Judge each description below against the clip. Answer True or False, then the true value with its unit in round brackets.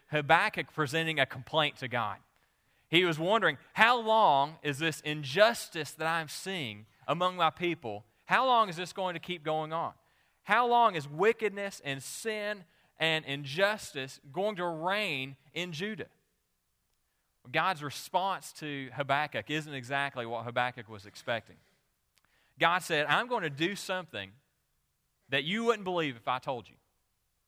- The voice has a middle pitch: True (155 Hz)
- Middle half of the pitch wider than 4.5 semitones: True (5.3 semitones)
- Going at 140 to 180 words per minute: True (145 wpm)